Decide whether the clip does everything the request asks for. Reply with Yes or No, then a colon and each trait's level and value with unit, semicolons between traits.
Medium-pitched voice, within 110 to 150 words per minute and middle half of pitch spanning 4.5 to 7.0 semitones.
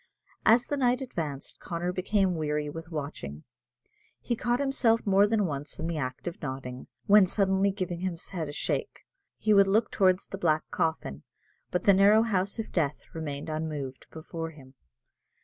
No: medium, 175 Hz; average, 170 wpm; average, 5.0 semitones